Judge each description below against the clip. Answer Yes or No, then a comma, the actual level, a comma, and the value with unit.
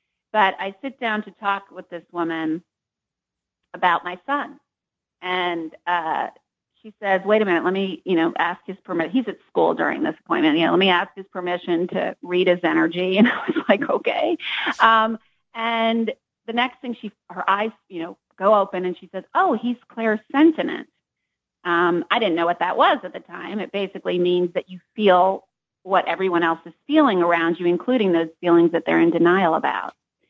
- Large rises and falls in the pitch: No, average, 4.3 semitones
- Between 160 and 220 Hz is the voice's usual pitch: Yes, medium, 185 Hz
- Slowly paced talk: No, average, 190 wpm